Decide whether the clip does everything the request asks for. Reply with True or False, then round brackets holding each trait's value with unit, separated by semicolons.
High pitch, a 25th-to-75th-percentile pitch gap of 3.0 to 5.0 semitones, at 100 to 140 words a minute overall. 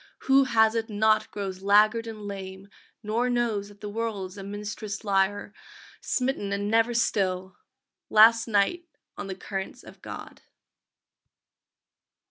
False (210 Hz; 2.4 semitones; 135 wpm)